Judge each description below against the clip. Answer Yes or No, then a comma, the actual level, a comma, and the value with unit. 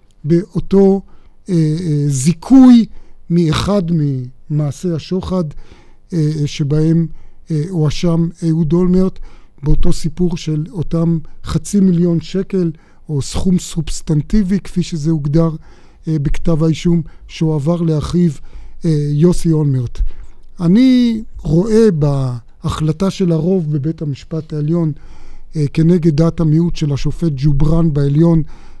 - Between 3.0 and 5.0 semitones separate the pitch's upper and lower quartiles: No, narrow, 2.5 semitones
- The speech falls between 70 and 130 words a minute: Yes, average, 105 wpm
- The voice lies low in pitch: No, medium, 165 Hz